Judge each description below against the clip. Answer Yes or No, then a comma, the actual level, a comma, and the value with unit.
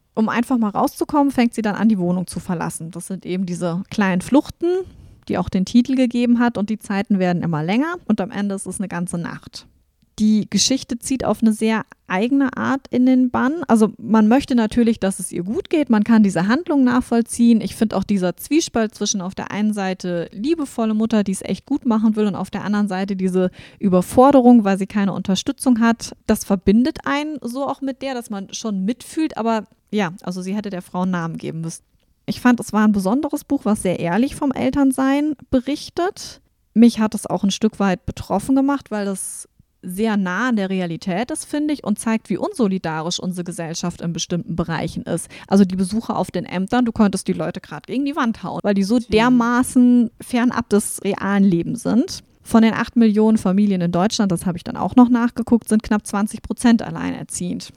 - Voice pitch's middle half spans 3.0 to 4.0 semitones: No, average, 4.5 semitones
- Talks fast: Yes, fast, 210 wpm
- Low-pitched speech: No, high, 215 Hz